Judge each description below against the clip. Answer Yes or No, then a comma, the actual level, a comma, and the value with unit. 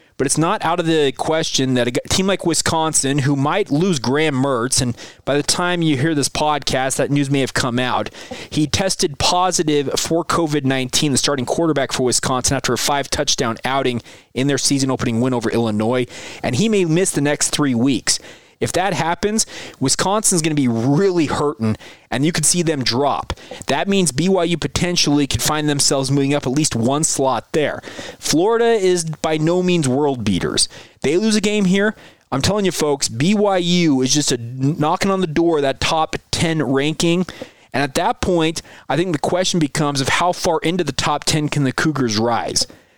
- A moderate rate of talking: Yes, average, 195 wpm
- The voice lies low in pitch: No, medium, 150 Hz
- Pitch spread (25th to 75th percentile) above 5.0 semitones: No, average, 4.3 semitones